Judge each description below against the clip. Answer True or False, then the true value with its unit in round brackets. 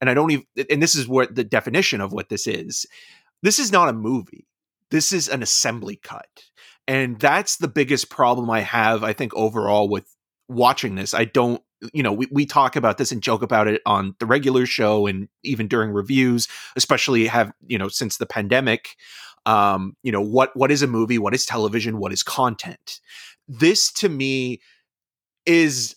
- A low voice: True (120 Hz)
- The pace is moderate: True (190 wpm)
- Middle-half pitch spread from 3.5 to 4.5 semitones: True (3.8 semitones)